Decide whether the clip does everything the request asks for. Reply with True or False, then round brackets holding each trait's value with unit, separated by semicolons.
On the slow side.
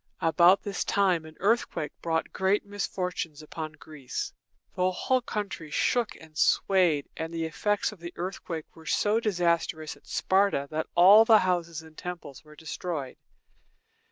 False (150 wpm)